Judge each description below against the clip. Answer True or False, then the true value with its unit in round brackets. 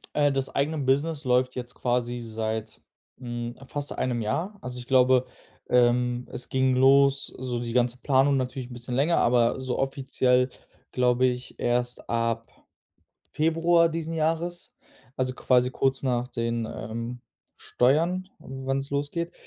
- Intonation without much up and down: True (2.3 semitones)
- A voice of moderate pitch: False (130 Hz)